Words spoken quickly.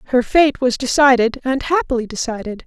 No: average, 160 wpm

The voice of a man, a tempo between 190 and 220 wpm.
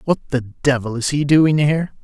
Yes: male; fast, 205 wpm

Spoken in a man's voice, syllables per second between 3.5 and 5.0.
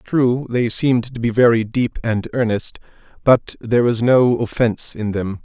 Yes: male; 4.7 syllables/s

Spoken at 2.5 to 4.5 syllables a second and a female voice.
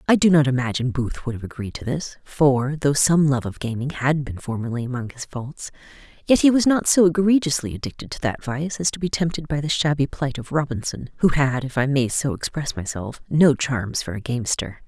No: 5.5 syllables/s; female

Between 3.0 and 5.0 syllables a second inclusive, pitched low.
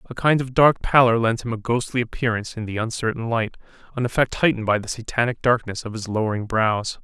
No: 6.2 syllables/s; low, 115 Hz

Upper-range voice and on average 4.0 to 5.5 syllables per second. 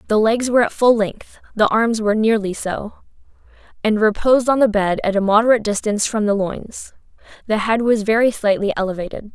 No: high, 215 Hz; 5.9 syllables/s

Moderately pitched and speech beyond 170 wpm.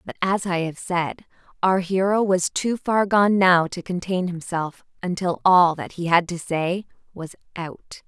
Yes: medium, 180 Hz; average, 180 wpm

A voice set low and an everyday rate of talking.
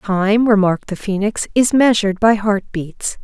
No: high, 205 Hz; average, 150 wpm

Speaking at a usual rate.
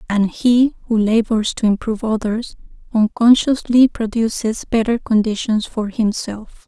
No: slow, 115 wpm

